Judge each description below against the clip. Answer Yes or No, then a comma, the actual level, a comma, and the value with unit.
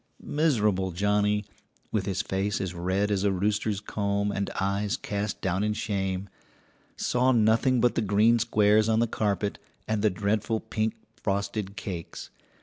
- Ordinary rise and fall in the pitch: No, narrow, 1.8 semitones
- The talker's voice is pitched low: Yes, low, 105 Hz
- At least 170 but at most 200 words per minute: No, average, 150 wpm